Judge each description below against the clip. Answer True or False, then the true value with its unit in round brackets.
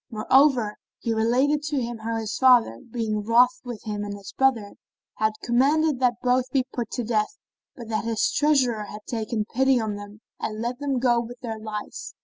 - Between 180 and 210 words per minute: True (190 wpm)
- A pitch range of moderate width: True (3.0 semitones)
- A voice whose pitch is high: True (235 Hz)